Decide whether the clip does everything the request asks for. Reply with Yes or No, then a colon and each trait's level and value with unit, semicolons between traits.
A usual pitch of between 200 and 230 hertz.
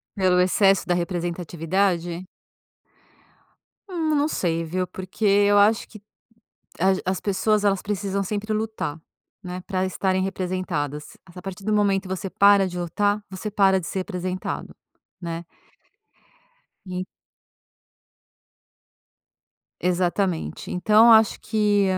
No: high, 190 Hz